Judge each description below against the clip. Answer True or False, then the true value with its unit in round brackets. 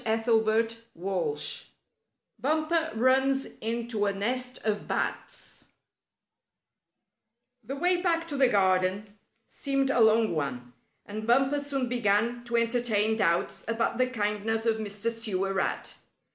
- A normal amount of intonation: True (3.8 semitones)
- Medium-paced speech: False (120 wpm)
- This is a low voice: False (225 Hz)